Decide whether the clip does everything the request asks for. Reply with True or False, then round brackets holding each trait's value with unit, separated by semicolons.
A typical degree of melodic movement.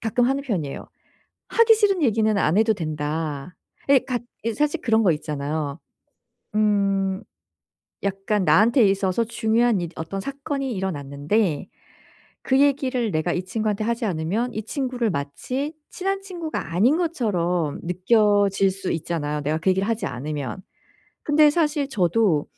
False (6.9 semitones)